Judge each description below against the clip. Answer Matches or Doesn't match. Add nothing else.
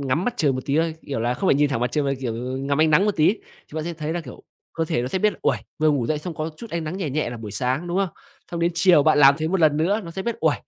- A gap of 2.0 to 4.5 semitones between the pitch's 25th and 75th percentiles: Matches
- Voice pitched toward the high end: Doesn't match